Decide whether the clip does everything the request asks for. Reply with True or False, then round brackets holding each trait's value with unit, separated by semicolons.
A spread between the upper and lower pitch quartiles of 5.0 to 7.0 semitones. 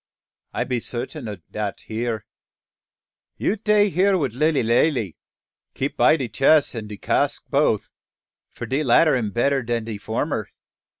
True (5.5 semitones)